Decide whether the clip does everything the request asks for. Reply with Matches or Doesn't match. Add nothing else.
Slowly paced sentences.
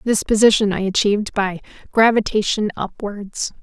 Matches